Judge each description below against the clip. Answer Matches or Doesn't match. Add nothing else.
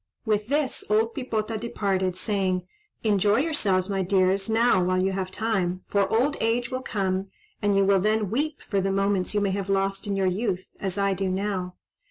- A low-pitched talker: Doesn't match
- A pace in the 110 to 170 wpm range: Doesn't match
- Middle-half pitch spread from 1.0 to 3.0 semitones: Matches